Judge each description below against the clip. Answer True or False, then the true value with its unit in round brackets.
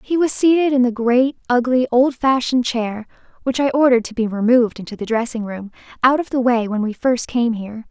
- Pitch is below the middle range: False (245 Hz)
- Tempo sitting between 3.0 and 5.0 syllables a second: False (5.7 syllables/s)